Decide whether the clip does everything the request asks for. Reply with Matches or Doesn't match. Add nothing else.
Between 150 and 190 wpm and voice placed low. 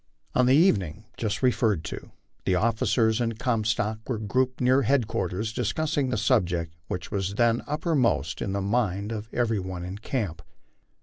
Matches